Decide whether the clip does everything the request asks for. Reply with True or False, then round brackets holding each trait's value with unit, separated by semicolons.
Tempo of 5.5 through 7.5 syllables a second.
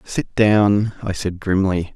False (3.4 syllables/s)